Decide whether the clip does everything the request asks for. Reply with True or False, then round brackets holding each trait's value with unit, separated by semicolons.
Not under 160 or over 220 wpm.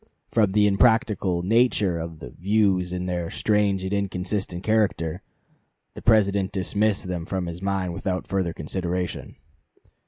False (135 wpm)